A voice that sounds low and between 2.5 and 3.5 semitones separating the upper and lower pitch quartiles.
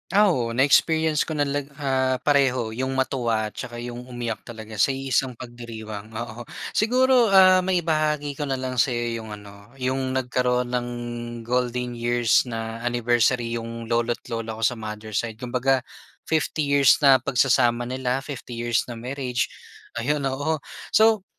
Yes: low, 125 Hz; average, 2.9 semitones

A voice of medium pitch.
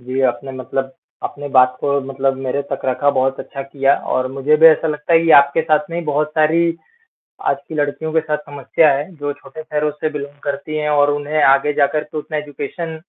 Yes: medium, 145 Hz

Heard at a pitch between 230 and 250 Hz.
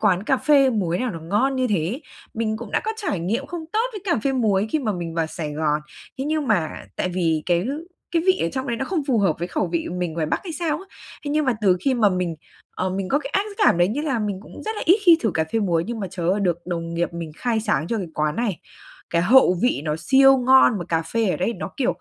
No: high, 210 Hz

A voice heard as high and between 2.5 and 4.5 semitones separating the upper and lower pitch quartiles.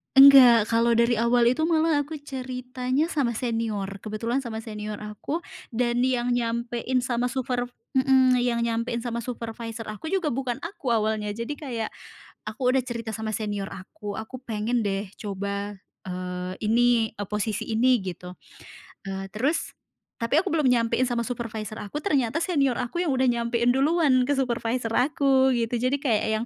Yes: high, 235 Hz; average, 2.9 semitones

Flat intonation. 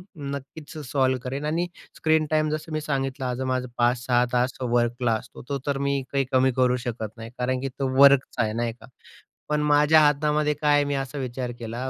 No: average, 3.1 semitones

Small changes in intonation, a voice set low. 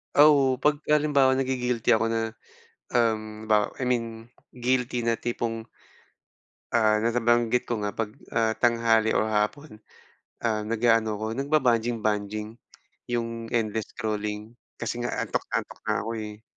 Yes: narrow, 2.0 semitones; low, 115 Hz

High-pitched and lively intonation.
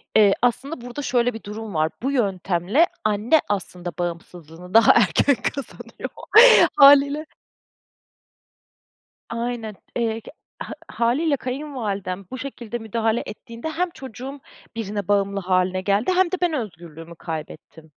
Yes: high, 225 Hz; wide, 5.8 semitones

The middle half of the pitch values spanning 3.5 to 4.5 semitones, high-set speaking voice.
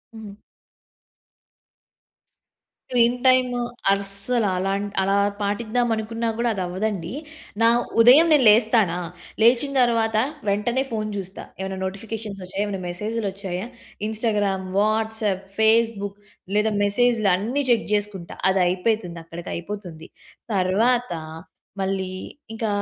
No: average, 3.0 semitones; high, 210 Hz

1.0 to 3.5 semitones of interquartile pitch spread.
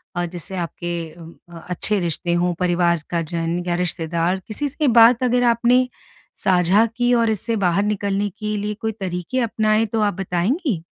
No: average, 4.5 semitones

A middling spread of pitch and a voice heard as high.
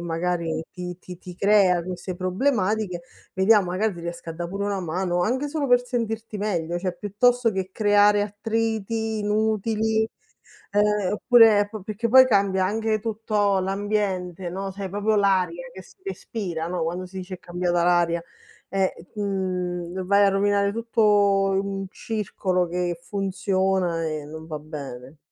Yes: average, 3.1 semitones; high, 195 Hz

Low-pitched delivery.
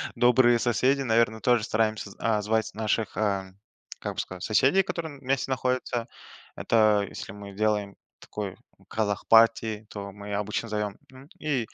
Yes: low, 110 Hz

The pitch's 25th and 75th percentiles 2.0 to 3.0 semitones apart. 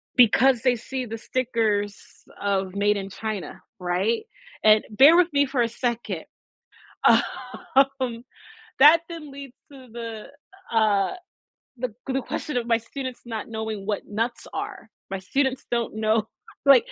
No: average, 3.7 semitones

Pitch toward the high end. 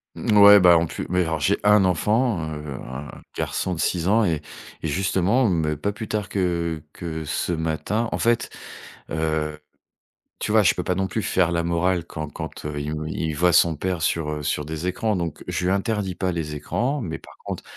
No: very low, 85 Hz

